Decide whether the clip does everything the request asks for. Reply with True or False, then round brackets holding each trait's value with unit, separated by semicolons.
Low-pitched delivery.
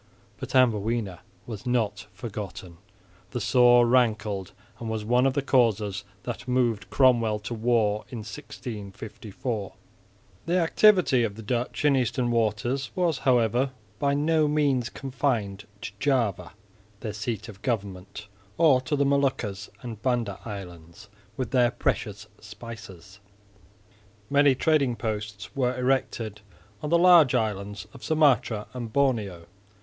True (120 Hz)